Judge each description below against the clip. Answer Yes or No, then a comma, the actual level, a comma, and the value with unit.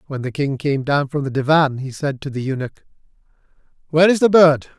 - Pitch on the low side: No, medium, 145 Hz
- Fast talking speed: Yes, fast, 215 wpm